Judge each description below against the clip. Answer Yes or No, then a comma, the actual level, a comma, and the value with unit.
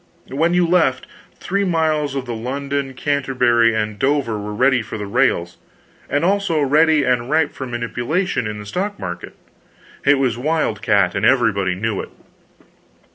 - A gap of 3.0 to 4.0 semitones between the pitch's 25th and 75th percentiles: No, average, 5.3 semitones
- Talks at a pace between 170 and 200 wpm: No, average, 155 wpm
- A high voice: No, low, 130 Hz